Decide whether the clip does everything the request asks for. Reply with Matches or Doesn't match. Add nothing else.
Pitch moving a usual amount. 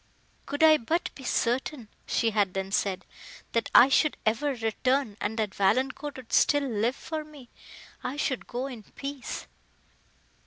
Matches